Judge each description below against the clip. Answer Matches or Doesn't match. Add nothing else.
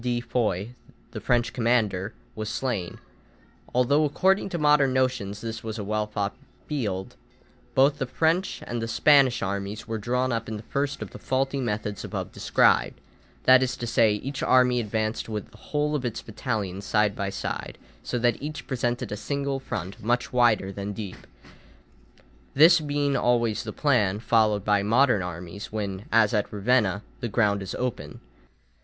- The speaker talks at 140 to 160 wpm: Doesn't match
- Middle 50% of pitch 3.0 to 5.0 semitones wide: Matches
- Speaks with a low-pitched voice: Matches